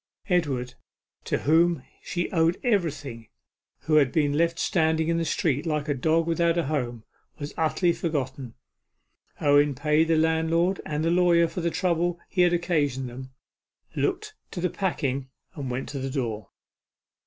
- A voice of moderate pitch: Yes, medium, 160 Hz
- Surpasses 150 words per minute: Yes, average, 160 wpm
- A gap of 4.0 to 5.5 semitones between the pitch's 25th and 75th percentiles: No, average, 3.5 semitones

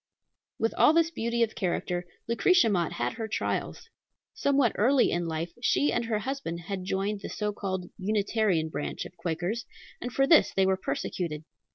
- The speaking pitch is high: Yes, high, 205 Hz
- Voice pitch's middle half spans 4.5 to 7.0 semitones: Yes, average, 4.9 semitones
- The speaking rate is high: No, average, 175 wpm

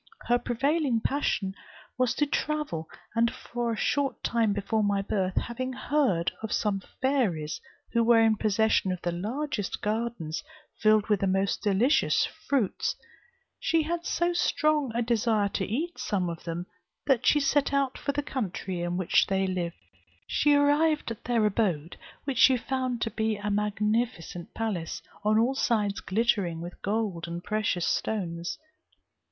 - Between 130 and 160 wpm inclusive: Yes, average, 155 wpm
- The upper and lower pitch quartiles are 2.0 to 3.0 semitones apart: No, average, 5.0 semitones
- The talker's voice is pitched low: No, high, 220 Hz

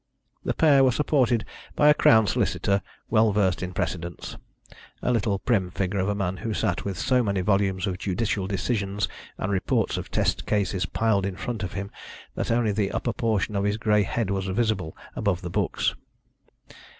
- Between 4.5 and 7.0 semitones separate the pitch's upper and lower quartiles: No, average, 2.9 semitones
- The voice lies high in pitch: No, low, 100 Hz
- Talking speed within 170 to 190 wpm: Yes, average, 185 wpm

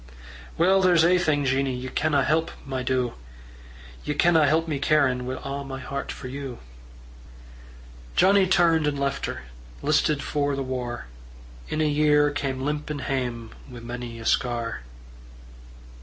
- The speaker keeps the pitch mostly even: No, average, 3.0 semitones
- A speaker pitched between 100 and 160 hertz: Yes, medium, 140 Hz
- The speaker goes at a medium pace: Yes, average, 150 wpm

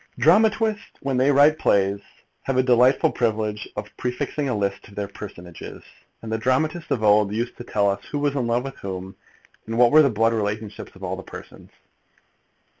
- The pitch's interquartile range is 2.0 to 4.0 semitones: No, average, 4.8 semitones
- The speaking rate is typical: Yes, average, 195 wpm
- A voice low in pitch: Yes, low, 115 Hz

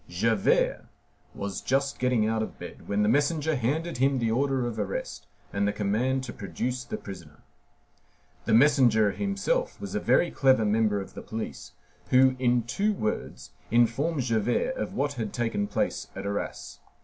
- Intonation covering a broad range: No, average, 4.4 semitones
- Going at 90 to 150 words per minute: No, average, 165 wpm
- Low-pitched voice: Yes, low, 120 Hz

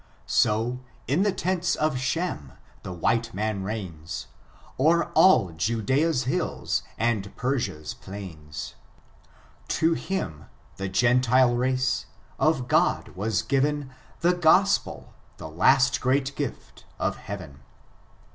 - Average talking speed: No, slow, 115 wpm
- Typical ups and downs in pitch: No, wide, 6.9 semitones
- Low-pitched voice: Yes, low, 125 Hz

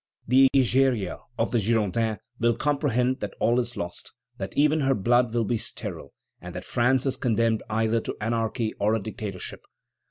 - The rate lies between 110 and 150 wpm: No, average, 170 wpm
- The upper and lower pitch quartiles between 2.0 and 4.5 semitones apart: Yes, average, 2.7 semitones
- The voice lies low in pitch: Yes, low, 115 Hz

